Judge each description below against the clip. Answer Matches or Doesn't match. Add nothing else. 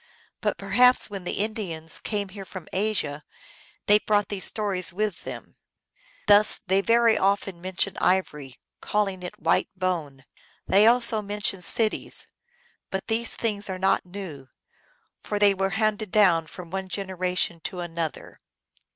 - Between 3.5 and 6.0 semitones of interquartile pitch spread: Doesn't match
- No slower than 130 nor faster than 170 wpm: Matches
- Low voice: Doesn't match